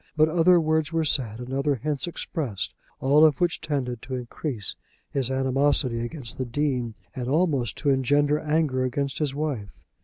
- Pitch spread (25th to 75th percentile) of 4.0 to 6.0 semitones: No, average, 3.3 semitones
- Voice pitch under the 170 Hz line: Yes, medium, 140 Hz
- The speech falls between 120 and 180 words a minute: Yes, average, 165 wpm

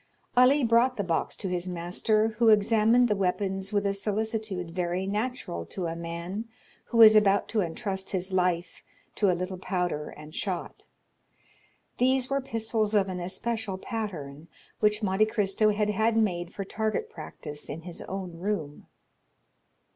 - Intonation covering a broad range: No, average, 3.5 semitones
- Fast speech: No, average, 155 wpm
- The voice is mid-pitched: No, high, 200 Hz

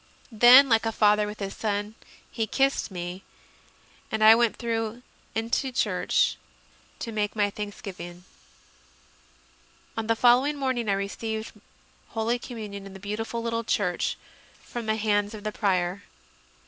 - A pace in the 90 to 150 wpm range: Yes, average, 145 wpm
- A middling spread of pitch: No, narrow, 2.3 semitones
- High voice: Yes, high, 220 Hz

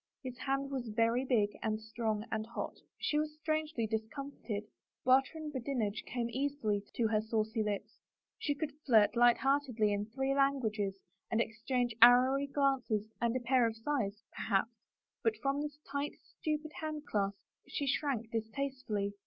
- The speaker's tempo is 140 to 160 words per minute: Yes, average, 155 wpm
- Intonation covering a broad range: No, average, 4.0 semitones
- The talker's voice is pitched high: Yes, high, 240 Hz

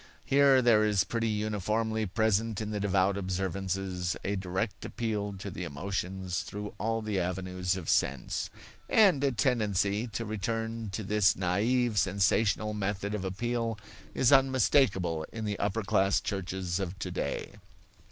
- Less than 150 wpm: Yes, average, 140 wpm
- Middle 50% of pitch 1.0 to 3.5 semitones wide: Yes, average, 2.9 semitones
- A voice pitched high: No, low, 100 Hz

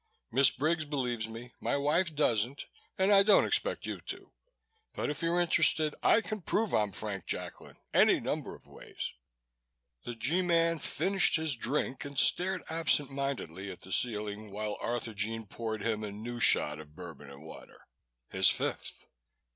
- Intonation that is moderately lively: No, wide, 7.2 semitones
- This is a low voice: Yes, low, 125 Hz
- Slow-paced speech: No, average, 165 wpm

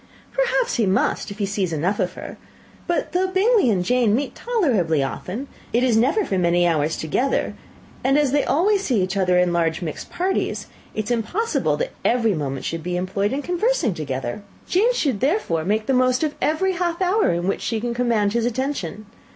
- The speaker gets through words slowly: No, average, 200 wpm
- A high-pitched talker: Yes, high, 230 Hz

